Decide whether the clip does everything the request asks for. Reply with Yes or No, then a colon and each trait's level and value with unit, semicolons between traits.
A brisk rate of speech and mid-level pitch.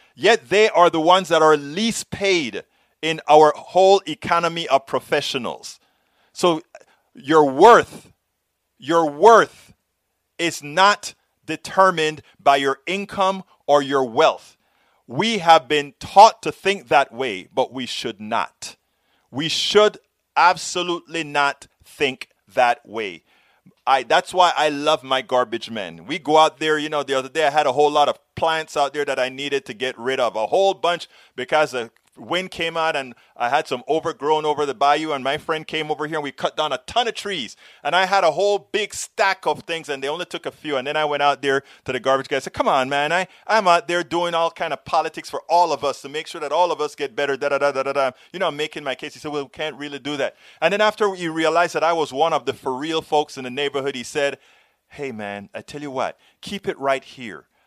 Yes: fast, 215 wpm; medium, 155 Hz